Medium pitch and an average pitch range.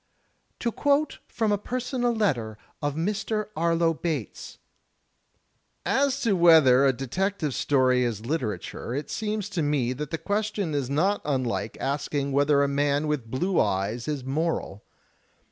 No: medium, 150 Hz; wide, 7.2 semitones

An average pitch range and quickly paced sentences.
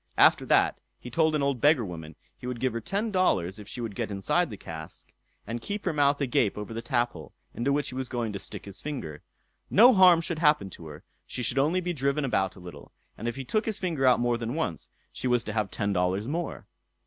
No: wide, 6.7 semitones; fast, 245 wpm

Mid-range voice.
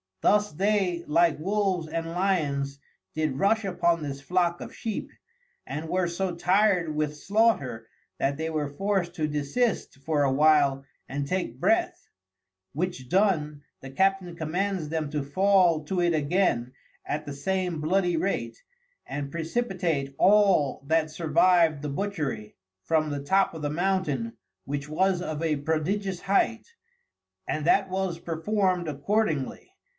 Yes: medium, 165 Hz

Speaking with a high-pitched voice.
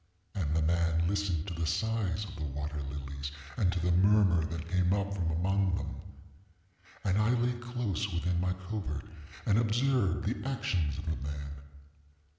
No: very low, 90 Hz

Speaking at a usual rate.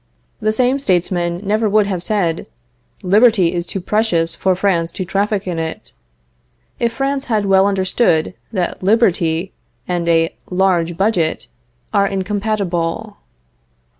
No: slow, 130 wpm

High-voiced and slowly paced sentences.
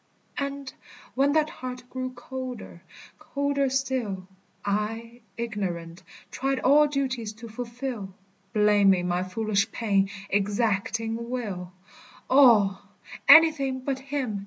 Yes: high, 235 Hz; slow, 105 wpm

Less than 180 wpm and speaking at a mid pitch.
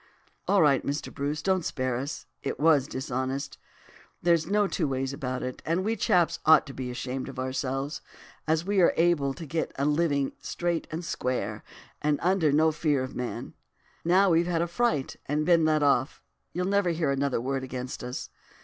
No: average, 185 wpm; medium, 150 Hz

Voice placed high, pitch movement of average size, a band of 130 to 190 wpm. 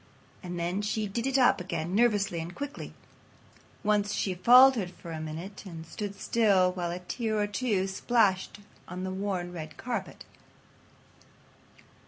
Yes: high, 195 Hz; average, 3.4 semitones; average, 150 wpm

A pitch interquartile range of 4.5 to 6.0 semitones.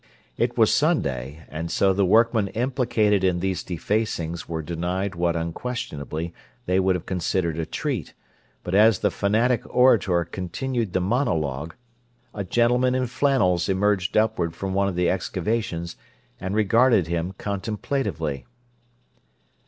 Yes: average, 4.8 semitones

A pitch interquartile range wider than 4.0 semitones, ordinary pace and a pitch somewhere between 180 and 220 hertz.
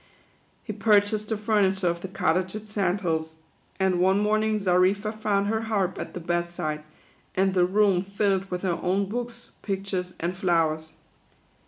No: average, 2.7 semitones; average, 165 wpm; high, 190 Hz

